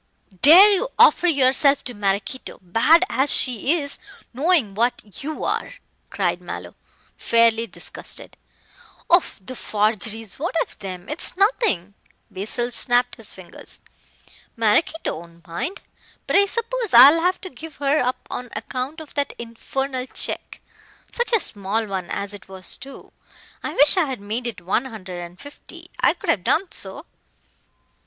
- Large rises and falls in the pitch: Yes, wide, 7.1 semitones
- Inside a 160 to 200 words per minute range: No, average, 150 wpm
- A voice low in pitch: No, very high, 250 Hz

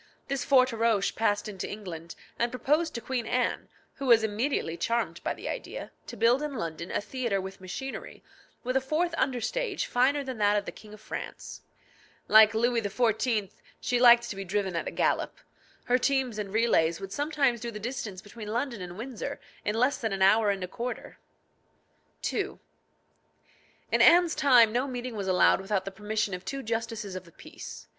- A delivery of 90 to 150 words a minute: No, average, 185 wpm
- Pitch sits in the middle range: No, high, 225 Hz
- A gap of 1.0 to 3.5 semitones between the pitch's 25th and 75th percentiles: No, average, 3.9 semitones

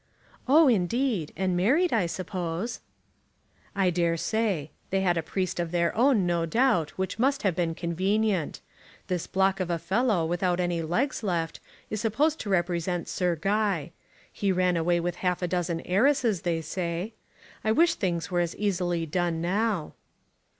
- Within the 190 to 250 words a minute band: No, average, 165 wpm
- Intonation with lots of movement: No, average, 3.8 semitones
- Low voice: No, medium, 180 Hz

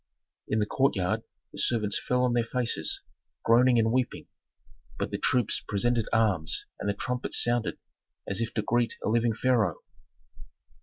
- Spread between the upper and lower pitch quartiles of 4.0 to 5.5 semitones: No, narrow, 2.6 semitones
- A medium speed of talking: Yes, average, 155 wpm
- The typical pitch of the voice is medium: No, low, 115 Hz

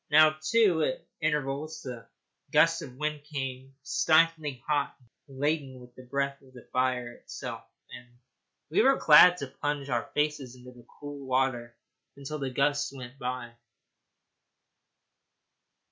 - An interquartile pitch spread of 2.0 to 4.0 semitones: Yes, average, 3.0 semitones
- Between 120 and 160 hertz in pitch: Yes, medium, 140 Hz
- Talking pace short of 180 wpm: Yes, average, 140 wpm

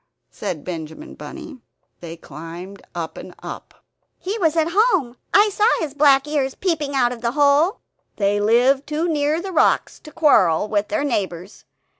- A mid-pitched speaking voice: No, very high, 275 Hz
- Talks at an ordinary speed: Yes, average, 165 wpm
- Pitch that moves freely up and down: Yes, wide, 7.8 semitones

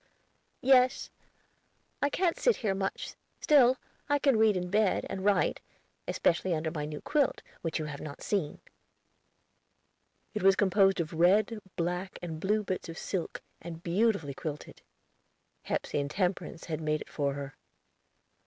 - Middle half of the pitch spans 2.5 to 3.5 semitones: No, average, 5.1 semitones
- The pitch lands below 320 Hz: Yes, medium, 185 Hz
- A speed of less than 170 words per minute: Yes, average, 150 wpm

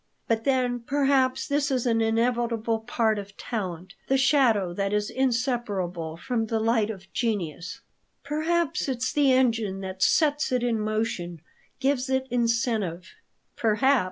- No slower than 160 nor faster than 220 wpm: No, average, 140 wpm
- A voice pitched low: No, high, 230 Hz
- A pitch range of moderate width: Yes, average, 4.0 semitones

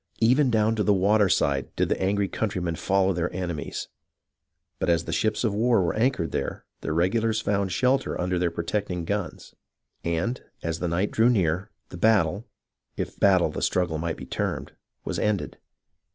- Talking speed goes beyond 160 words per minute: Yes, average, 175 wpm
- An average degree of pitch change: Yes, average, 4.0 semitones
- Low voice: Yes, very low, 95 Hz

